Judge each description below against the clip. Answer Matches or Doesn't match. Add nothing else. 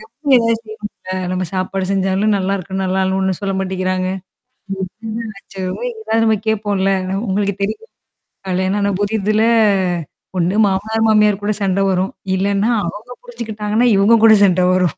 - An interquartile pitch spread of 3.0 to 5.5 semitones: Doesn't match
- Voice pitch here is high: Matches